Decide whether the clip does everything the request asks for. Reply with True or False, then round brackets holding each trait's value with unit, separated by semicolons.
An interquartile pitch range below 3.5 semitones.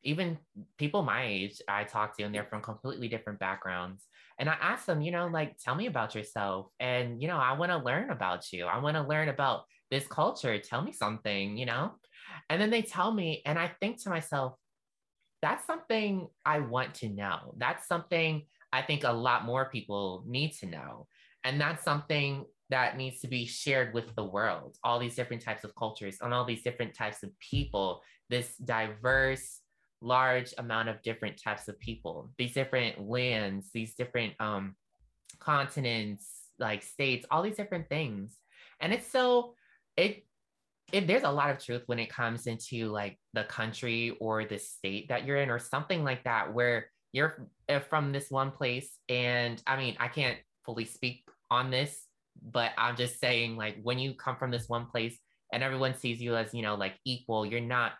False (4.3 semitones)